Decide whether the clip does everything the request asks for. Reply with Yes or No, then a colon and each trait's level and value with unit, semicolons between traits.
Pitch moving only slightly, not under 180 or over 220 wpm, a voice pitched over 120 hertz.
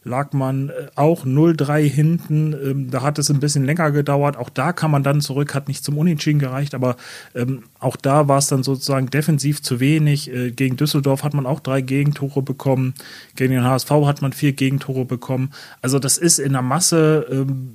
Yes: narrow, 1.9 semitones; average, 185 wpm; medium, 140 Hz